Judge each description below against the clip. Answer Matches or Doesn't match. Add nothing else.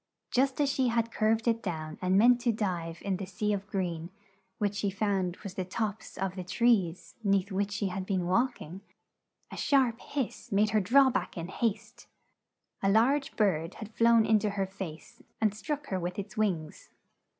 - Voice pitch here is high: Matches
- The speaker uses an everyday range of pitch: Matches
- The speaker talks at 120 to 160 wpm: Doesn't match